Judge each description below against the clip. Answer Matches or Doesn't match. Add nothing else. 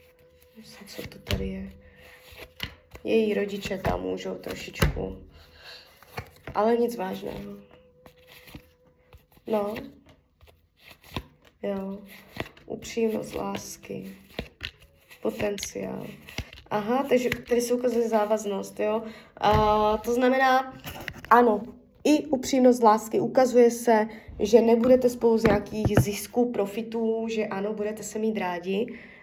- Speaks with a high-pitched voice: Matches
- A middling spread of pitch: Matches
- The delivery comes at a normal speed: Doesn't match